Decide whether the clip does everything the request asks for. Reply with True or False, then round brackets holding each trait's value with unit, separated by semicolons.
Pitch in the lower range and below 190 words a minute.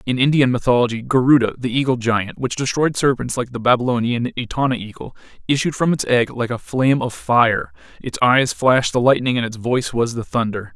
False (125 Hz; 195 wpm)